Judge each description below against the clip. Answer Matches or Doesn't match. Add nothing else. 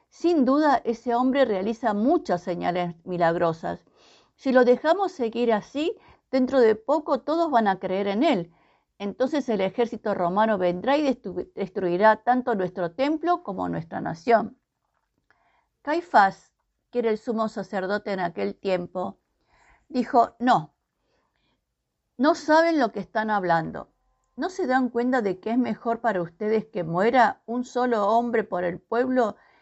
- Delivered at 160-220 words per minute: Doesn't match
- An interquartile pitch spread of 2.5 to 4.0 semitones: Doesn't match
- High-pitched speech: Matches